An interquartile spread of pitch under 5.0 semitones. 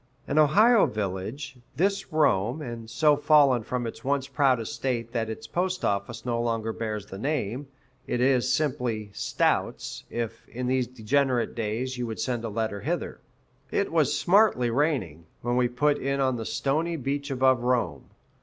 Yes: average, 3.9 semitones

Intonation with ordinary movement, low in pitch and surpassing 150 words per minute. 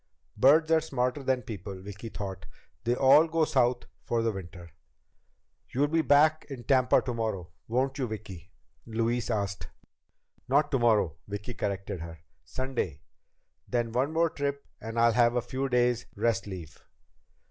No: average, 4.8 semitones; low, 120 Hz; average, 145 wpm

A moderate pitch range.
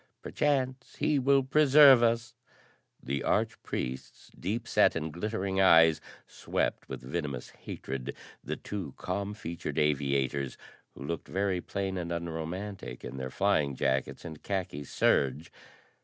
No: wide, 6.8 semitones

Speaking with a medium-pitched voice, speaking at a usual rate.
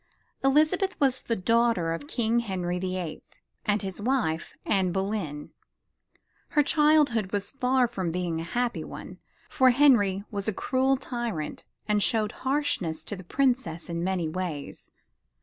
No: high, 210 Hz; average, 150 wpm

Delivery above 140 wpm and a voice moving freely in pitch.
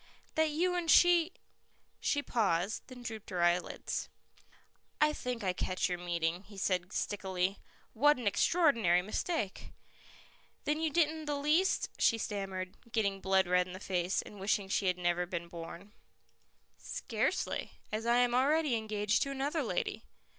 Yes: average, 160 wpm; wide, 7.8 semitones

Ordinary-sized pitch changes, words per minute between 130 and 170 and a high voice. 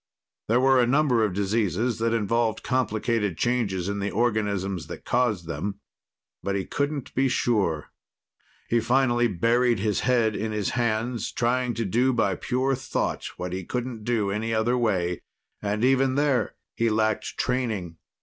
No: average, 3.5 semitones; average, 160 wpm; low, 115 Hz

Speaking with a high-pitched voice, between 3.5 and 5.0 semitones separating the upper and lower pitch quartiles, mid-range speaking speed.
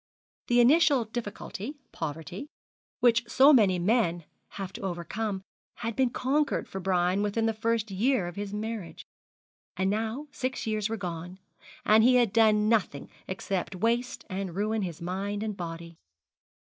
Yes: high, 210 Hz; average, 3.8 semitones; average, 150 wpm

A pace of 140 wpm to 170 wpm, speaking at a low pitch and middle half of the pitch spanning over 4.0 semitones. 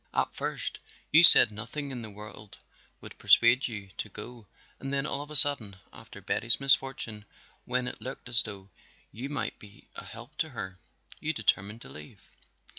No: average, 180 wpm; low, 115 Hz; average, 4.4 semitones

